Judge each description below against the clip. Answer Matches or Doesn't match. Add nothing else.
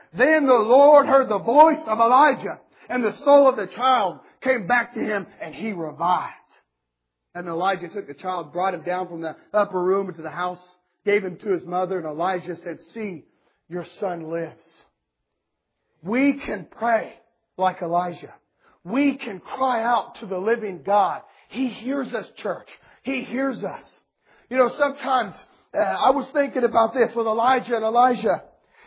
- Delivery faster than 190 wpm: Doesn't match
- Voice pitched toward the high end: Matches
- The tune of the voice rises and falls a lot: Matches